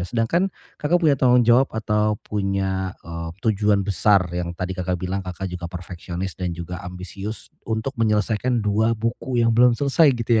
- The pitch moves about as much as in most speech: Yes, average, 4.1 semitones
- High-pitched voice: No, low, 105 Hz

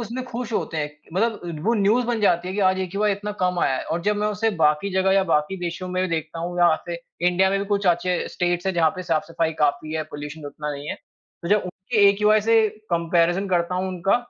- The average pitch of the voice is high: No, medium, 180 Hz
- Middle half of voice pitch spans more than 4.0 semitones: No, average, 3.3 semitones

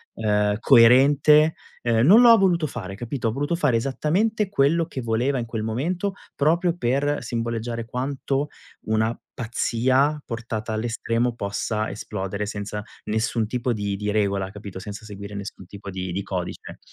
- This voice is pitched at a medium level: No, low, 115 Hz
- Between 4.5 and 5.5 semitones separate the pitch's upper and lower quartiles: Yes, average, 5.1 semitones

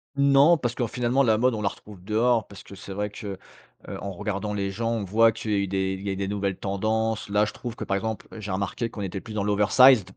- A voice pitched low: Yes, low, 105 Hz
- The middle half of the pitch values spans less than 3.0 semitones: Yes, narrow, 2.6 semitones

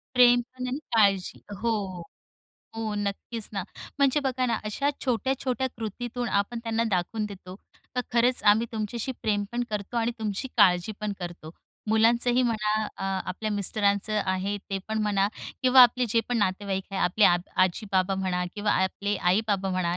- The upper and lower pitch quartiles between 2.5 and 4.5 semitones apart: Yes, average, 3.4 semitones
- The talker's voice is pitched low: No, high, 215 Hz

